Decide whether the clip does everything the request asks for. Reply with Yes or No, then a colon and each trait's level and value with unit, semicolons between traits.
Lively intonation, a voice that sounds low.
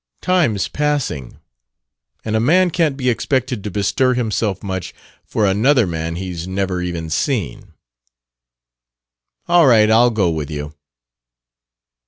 Yes: wide, 6.4 semitones; low, 105 Hz